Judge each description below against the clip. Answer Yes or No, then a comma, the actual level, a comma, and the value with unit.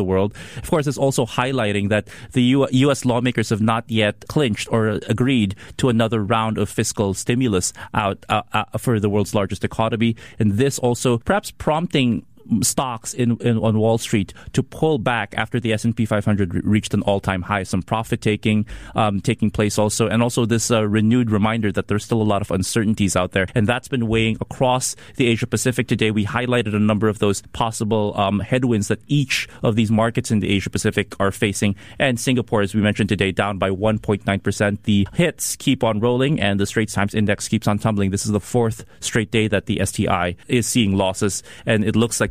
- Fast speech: Yes, fast, 210 wpm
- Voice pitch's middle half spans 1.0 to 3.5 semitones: Yes, average, 2.7 semitones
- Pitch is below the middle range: Yes, low, 110 Hz